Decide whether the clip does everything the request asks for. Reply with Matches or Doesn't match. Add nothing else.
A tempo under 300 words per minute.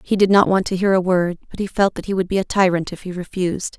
Doesn't match